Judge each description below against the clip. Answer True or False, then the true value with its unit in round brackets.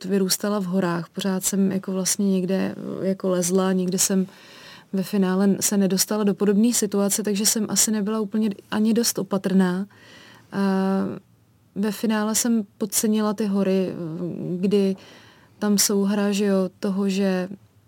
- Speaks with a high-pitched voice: True (195 Hz)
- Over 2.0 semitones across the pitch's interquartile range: False (1.7 semitones)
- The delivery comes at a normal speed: True (140 wpm)